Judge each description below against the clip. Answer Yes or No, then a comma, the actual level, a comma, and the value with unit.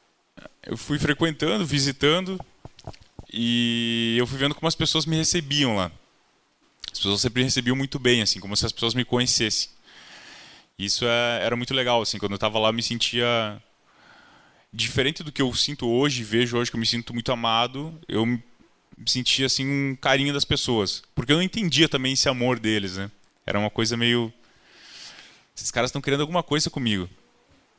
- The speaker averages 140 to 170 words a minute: No, average, 180 wpm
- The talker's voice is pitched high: No, low, 125 Hz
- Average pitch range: Yes, average, 3.5 semitones